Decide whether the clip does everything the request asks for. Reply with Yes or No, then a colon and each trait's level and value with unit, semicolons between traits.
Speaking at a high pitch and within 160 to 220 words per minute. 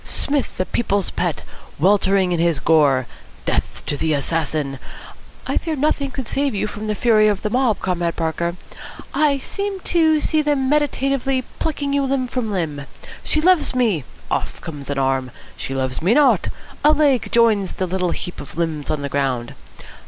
Yes: high, 205 Hz; average, 175 wpm